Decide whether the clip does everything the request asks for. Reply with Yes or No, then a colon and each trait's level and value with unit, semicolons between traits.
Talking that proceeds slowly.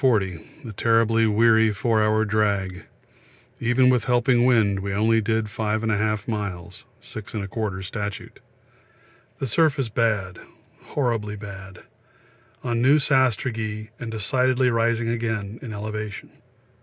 Yes: slow, 120 wpm